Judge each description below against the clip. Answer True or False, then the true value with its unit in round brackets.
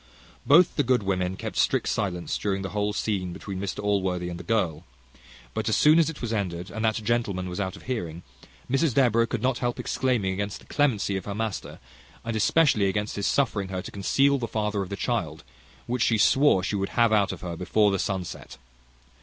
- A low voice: True (105 Hz)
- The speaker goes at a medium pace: False (215 wpm)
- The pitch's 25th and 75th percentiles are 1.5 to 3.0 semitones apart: False (3.8 semitones)